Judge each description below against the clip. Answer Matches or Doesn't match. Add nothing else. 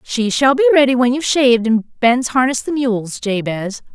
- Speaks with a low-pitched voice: Doesn't match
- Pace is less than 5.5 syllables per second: Matches